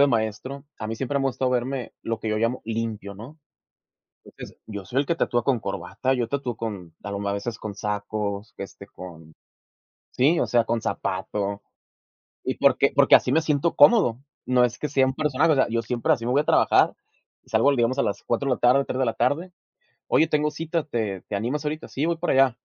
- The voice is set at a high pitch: No, low, 120 Hz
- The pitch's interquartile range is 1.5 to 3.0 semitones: No, average, 4.6 semitones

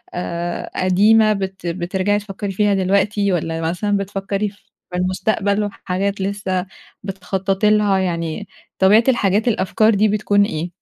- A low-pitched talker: No, high, 195 Hz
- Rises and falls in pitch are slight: Yes, narrow, 1.9 semitones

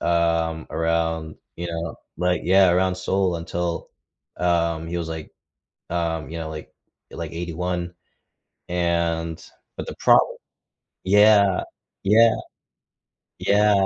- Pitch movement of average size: No, narrow, 1.8 semitones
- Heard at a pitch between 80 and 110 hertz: Yes, very low, 85 Hz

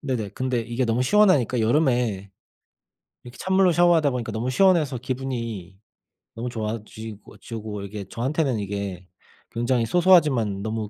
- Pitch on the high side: No, low, 120 Hz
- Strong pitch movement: No, average, 3.9 semitones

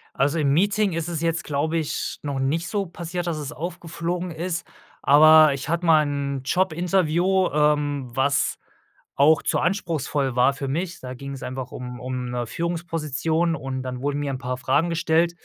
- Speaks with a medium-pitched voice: Yes, medium, 155 Hz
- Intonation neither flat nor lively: Yes, average, 3.6 semitones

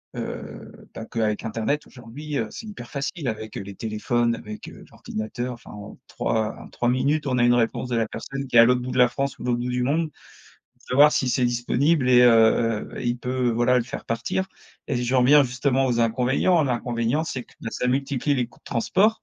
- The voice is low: Yes, low, 125 Hz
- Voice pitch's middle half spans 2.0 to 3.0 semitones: Yes, average, 2.7 semitones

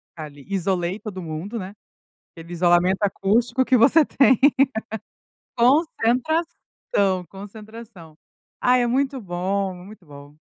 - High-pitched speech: Yes, high, 200 Hz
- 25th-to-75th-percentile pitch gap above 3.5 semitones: Yes, wide, 5.5 semitones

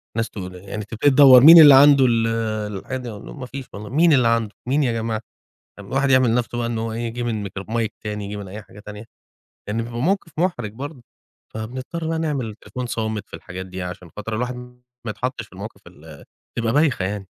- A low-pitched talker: Yes, low, 115 Hz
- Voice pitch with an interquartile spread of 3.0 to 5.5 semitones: Yes, average, 3.9 semitones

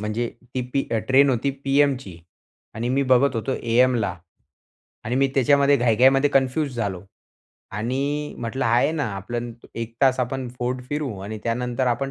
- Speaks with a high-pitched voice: No, low, 125 Hz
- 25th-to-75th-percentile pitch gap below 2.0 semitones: No, average, 2.9 semitones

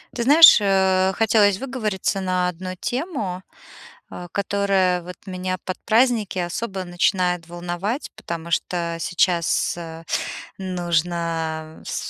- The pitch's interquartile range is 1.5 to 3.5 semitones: Yes, narrow, 2.6 semitones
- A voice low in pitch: No, medium, 185 Hz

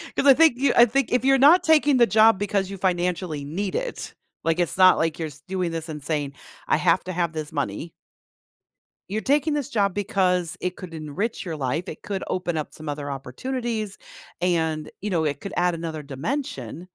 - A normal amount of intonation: No, wide, 6.0 semitones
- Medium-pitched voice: Yes, medium, 180 Hz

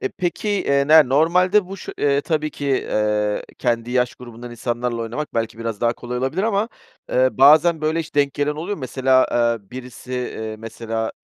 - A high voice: No, low, 130 Hz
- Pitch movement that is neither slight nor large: Yes, average, 4.7 semitones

